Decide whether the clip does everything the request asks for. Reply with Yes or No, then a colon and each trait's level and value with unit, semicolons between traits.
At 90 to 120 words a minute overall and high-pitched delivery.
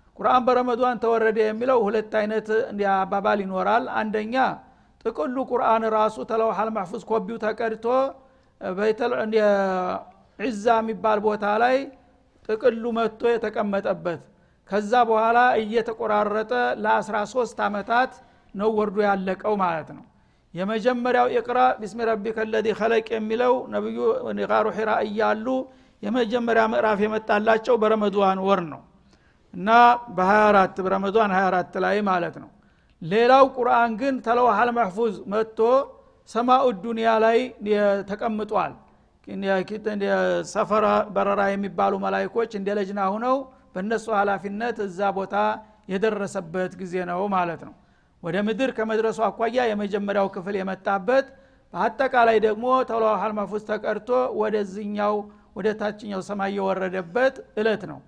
Yes: average, 105 wpm; high, 215 Hz